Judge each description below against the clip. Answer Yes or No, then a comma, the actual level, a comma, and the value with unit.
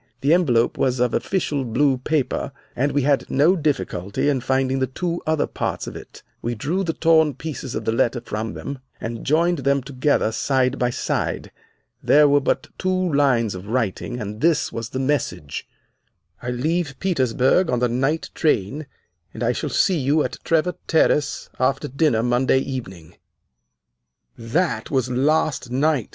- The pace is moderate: Yes, average, 165 wpm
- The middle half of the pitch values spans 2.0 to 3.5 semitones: No, average, 4.0 semitones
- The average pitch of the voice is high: No, low, 135 Hz